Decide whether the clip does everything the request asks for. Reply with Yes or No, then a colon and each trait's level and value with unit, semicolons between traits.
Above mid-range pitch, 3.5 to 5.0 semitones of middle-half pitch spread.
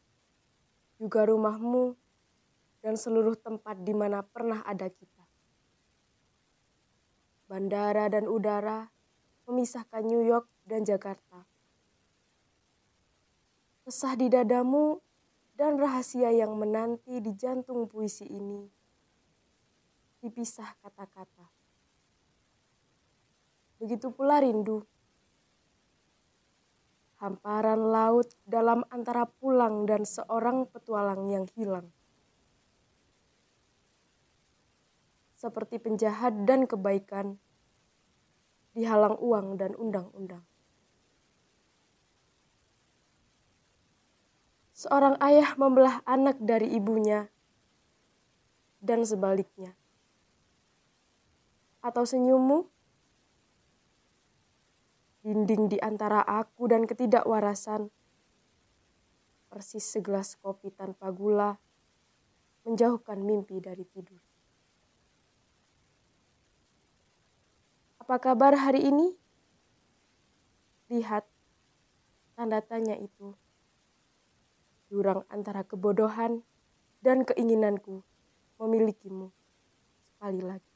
No: high, 220 Hz; average, 2.9 semitones